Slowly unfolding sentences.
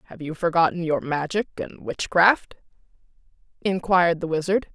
Yes: slow, 125 wpm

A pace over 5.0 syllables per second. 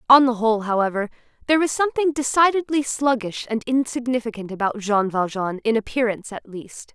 Yes: 5.9 syllables/s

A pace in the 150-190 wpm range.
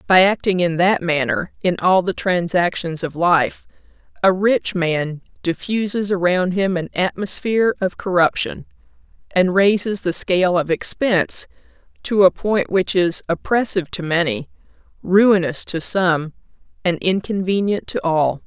No: slow, 135 wpm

